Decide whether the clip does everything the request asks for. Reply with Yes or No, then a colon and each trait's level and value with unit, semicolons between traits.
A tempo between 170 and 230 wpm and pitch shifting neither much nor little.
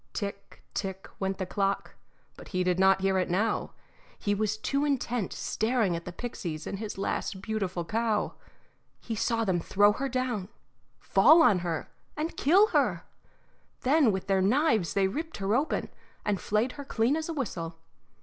Yes: average, 175 wpm; average, 4.7 semitones